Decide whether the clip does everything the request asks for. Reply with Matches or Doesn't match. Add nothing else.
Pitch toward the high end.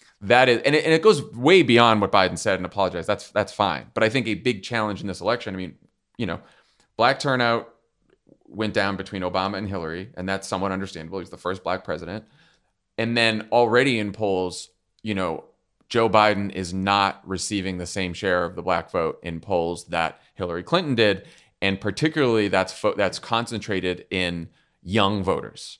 Doesn't match